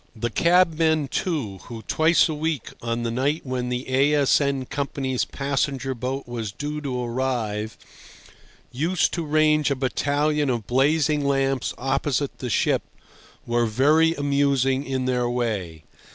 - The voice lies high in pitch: No, low, 135 Hz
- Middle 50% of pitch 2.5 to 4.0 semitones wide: Yes, average, 3.3 semitones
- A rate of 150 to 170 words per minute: No, average, 140 wpm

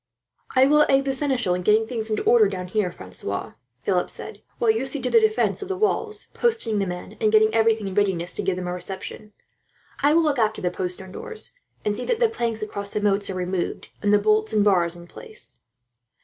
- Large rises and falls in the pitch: Yes, wide, 5.8 semitones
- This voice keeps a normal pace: No, fast, 225 wpm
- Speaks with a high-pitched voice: Yes, high, 215 Hz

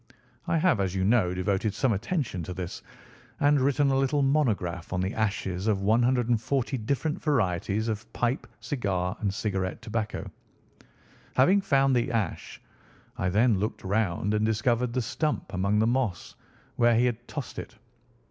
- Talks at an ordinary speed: Yes, average, 155 wpm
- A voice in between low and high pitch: No, low, 110 Hz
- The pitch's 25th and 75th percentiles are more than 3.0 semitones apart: Yes, average, 4.9 semitones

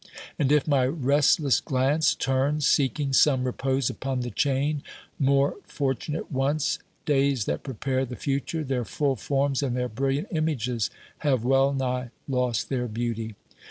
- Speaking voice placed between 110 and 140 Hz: Yes, low, 135 Hz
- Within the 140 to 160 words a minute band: Yes, average, 145 wpm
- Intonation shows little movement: Yes, narrow, 2.1 semitones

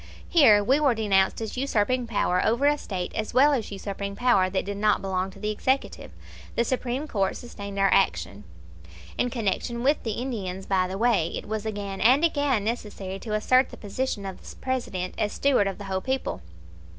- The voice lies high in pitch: Yes, high, 210 Hz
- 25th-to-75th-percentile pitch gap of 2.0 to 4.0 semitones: No, average, 4.6 semitones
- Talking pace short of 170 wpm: No, average, 195 wpm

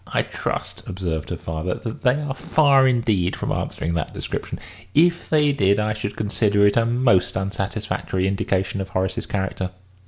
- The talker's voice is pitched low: Yes, low, 100 Hz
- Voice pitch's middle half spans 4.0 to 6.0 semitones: Yes, average, 4.7 semitones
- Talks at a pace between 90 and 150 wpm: No, average, 165 wpm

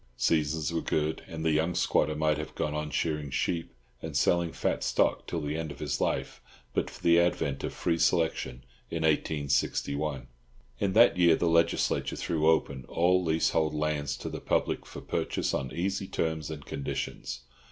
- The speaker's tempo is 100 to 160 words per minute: No, average, 175 wpm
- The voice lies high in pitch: No, very low, 80 Hz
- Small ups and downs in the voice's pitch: Yes, narrow, 1.9 semitones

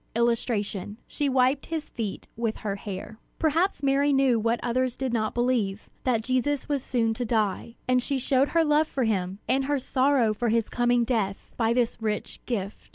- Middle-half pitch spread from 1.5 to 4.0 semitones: Yes, average, 3.4 semitones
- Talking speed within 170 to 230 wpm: Yes, average, 185 wpm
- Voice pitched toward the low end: No, high, 240 Hz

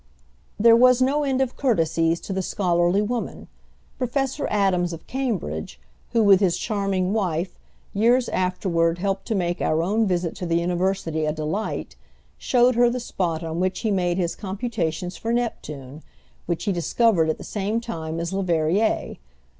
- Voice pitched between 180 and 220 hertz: Yes, high, 190 Hz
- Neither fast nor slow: Yes, average, 160 wpm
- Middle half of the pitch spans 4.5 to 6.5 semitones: Yes, average, 5.1 semitones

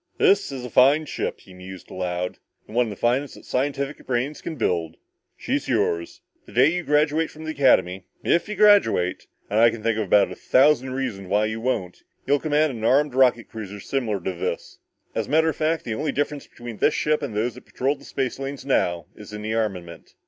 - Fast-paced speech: Yes, fast, 215 wpm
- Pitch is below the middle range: Yes, low, 125 Hz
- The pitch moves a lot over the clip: Yes, wide, 5.8 semitones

